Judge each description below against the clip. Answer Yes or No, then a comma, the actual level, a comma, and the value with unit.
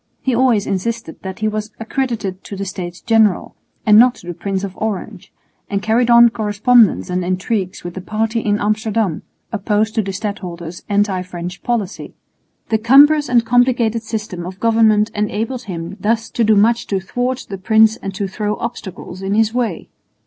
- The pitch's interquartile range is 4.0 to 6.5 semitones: No, average, 3.1 semitones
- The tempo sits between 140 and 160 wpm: No, average, 180 wpm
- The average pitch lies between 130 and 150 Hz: No, high, 215 Hz